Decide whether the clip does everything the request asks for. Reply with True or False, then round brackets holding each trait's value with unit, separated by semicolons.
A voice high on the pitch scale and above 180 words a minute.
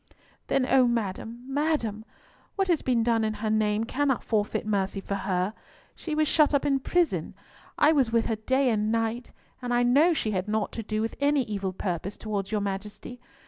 True (225 Hz; 195 wpm)